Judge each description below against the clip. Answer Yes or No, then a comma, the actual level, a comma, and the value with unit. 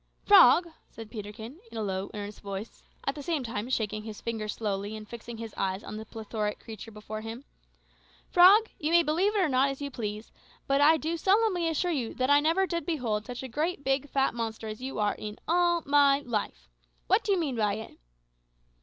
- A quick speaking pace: Yes, fast, 210 wpm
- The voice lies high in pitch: Yes, high, 245 Hz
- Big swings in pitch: Yes, wide, 6.5 semitones